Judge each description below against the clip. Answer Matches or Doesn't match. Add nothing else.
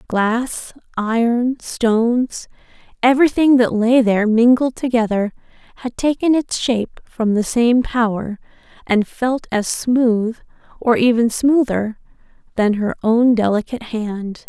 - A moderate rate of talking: Doesn't match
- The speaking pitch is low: Doesn't match